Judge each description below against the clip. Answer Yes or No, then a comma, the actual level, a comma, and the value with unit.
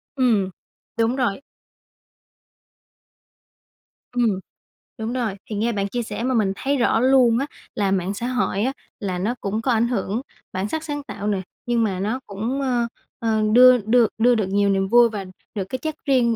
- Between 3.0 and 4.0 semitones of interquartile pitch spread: Yes, average, 3.6 semitones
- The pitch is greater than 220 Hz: Yes, high, 230 Hz